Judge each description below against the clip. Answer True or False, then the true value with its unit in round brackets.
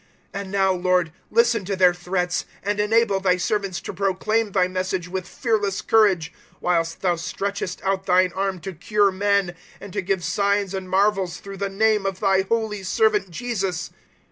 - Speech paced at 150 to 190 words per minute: True (180 wpm)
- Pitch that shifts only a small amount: True (1.9 semitones)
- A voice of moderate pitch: False (195 Hz)